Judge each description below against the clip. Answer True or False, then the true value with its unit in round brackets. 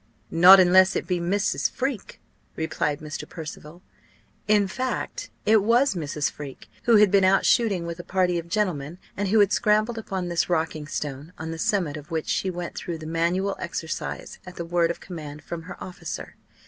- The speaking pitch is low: False (175 Hz)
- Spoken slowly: False (185 wpm)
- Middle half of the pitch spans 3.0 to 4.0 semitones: True (3.6 semitones)